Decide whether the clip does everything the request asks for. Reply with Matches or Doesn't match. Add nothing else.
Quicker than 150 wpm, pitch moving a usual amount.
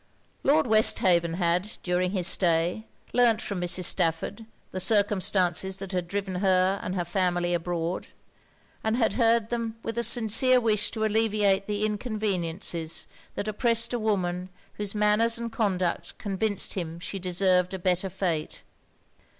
Doesn't match